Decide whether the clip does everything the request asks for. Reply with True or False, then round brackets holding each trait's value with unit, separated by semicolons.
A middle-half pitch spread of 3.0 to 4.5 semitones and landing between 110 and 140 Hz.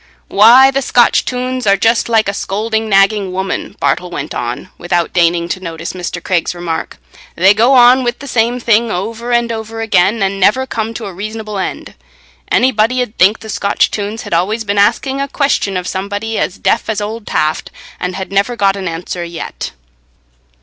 False (3.8 semitones; 210 Hz)